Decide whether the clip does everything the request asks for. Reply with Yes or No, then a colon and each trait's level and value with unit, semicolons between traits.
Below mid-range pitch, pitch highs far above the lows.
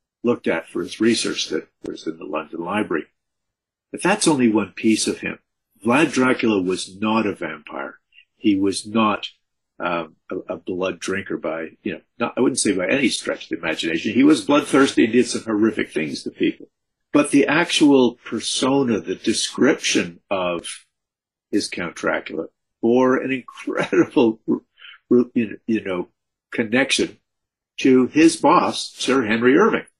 No: low, 120 Hz; average, 3.9 semitones